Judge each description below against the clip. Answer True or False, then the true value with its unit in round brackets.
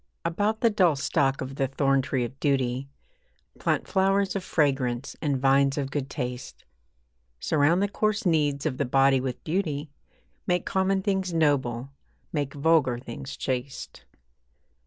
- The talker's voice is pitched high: False (140 Hz)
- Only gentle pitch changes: False (4.2 semitones)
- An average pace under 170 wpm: True (140 wpm)